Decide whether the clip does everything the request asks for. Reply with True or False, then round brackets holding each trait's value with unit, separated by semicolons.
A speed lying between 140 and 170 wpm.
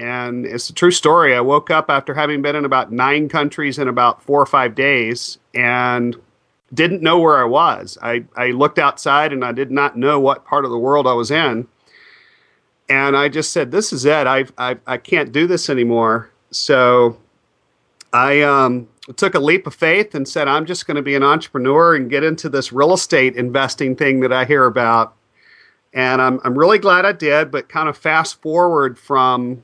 False (200 wpm)